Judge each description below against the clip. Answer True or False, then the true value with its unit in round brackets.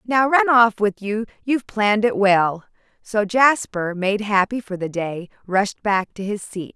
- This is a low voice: False (210 Hz)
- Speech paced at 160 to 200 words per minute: True (185 wpm)